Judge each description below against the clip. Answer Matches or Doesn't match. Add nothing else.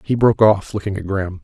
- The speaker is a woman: Doesn't match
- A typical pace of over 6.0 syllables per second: Matches